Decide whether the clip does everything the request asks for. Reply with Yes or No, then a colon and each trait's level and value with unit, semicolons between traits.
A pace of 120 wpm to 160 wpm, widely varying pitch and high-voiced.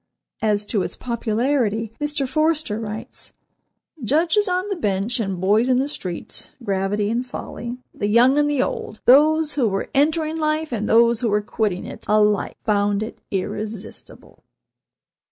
Yes: average, 155 wpm; wide, 5.8 semitones; high, 230 Hz